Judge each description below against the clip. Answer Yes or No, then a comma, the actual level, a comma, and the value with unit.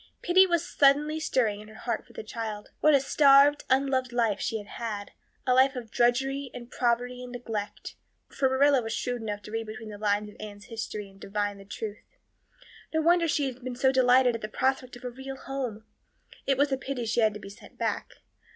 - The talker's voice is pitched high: Yes, high, 245 Hz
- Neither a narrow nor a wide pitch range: Yes, average, 3.9 semitones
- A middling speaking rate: No, fast, 215 wpm